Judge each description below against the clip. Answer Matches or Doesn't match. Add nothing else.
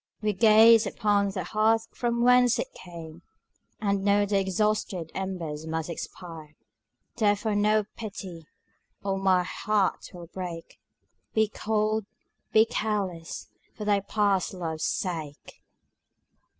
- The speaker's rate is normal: Doesn't match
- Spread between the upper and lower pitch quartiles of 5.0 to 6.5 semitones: Doesn't match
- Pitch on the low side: Doesn't match